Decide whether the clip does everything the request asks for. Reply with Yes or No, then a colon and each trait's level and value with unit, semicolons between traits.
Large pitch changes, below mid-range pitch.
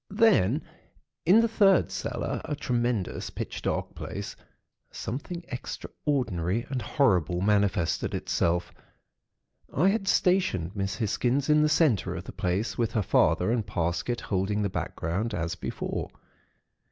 Yes: wide, 8.1 semitones; low, 115 Hz